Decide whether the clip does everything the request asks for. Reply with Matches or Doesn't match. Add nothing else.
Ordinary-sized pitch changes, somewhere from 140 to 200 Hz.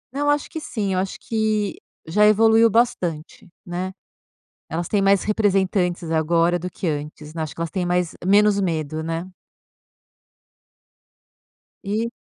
Matches